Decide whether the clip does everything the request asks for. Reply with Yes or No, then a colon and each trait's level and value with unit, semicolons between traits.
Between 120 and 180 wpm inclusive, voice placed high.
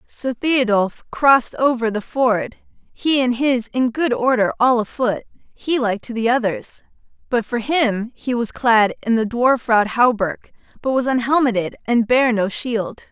Yes: average, 170 wpm; high, 240 Hz